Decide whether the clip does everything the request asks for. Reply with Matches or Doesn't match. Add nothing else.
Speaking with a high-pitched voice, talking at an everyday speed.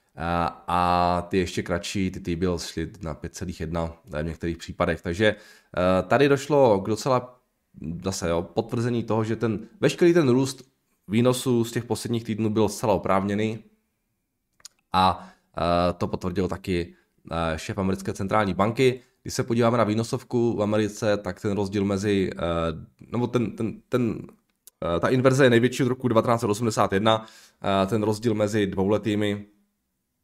Doesn't match